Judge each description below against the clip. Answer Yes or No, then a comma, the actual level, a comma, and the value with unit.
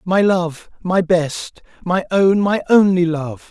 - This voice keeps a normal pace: Yes, average, 155 wpm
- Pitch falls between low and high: Yes, medium, 180 Hz